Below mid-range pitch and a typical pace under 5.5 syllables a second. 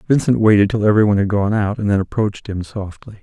No: low, 105 Hz; 6.6 syllables/s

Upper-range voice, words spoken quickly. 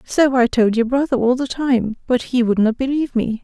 Yes: very high, 250 Hz; fast, 225 wpm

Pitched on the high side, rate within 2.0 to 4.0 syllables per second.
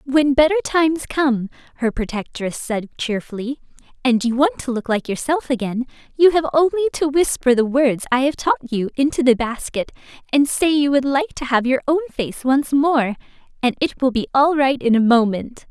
No: very high, 265 Hz; 5.1 syllables/s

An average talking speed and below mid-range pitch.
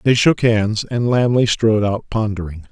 Yes: average, 175 wpm; low, 110 Hz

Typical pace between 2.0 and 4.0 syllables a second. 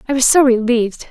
No: 6.5 syllables/s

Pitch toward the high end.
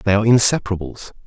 No: low, 105 Hz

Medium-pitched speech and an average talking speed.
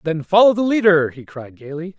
No: medium, 170 Hz; fast, 210 wpm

